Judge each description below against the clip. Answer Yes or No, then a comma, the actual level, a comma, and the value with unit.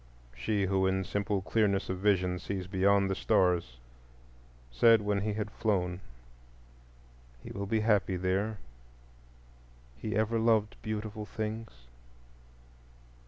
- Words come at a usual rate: No, slow, 120 wpm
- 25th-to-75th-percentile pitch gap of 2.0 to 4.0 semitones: Yes, narrow, 2.4 semitones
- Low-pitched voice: Yes, low, 100 Hz